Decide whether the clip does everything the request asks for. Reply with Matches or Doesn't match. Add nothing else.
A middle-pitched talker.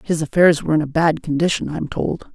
Matches